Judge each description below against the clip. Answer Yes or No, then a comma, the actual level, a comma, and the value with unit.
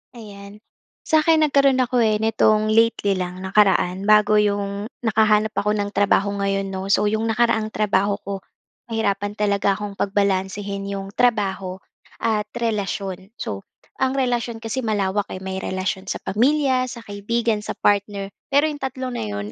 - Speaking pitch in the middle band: No, high, 210 Hz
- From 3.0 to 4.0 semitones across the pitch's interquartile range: No, narrow, 2.5 semitones